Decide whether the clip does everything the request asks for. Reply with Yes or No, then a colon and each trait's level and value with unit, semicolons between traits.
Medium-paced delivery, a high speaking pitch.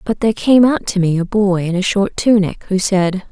No: fast, 255 wpm; high, 200 Hz